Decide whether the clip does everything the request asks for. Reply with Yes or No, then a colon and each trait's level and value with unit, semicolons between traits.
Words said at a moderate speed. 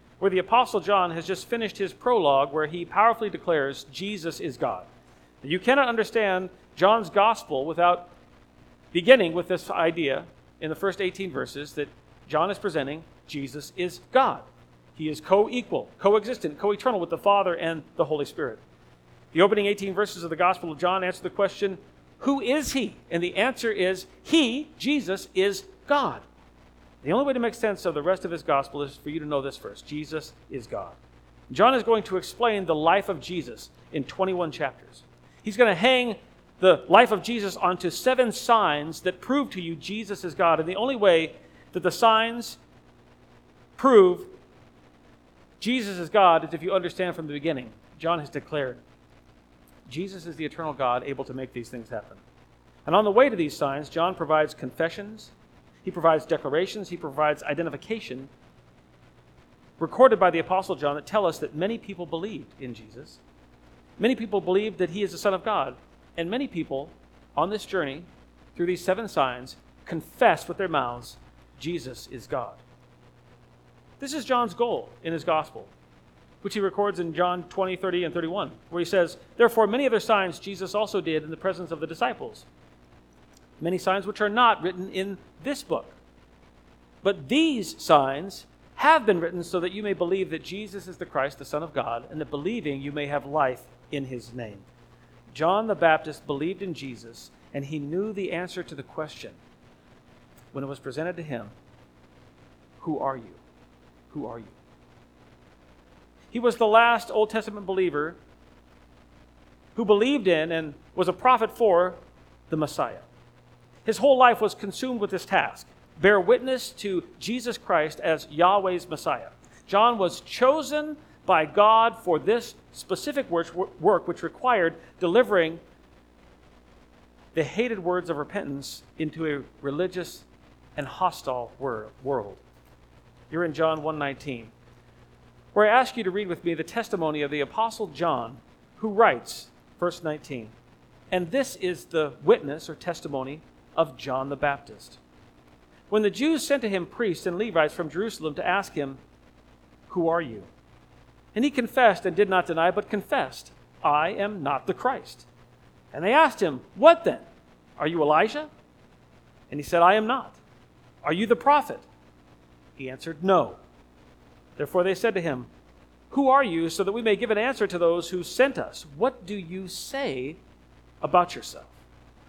Yes: average, 170 wpm